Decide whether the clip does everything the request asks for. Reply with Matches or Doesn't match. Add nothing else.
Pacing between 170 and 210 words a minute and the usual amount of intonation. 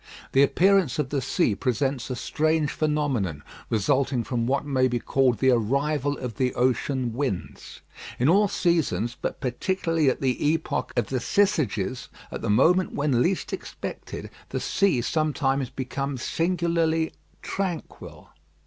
Doesn't match